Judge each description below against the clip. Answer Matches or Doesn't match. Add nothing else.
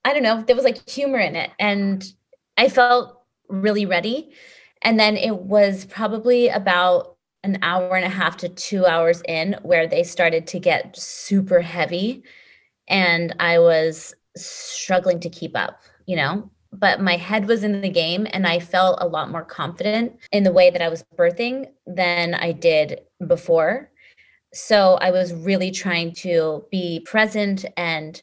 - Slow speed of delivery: Doesn't match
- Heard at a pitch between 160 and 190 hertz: Matches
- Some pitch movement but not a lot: Matches